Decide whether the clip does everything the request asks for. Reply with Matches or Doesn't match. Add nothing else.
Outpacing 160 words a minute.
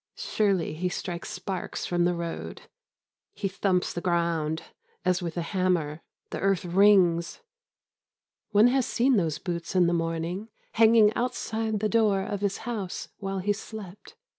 Doesn't match